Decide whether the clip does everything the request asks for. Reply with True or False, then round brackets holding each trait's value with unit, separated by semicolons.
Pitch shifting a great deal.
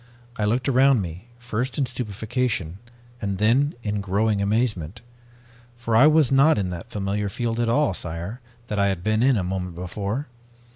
False (4.2 semitones)